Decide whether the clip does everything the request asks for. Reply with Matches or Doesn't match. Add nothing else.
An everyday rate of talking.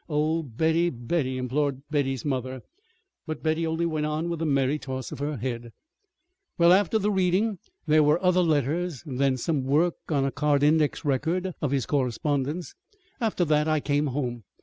Matches